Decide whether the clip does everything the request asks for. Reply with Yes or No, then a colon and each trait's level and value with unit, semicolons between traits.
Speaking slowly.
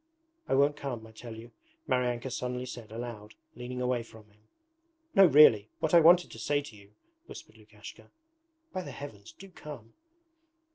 No: average, 175 wpm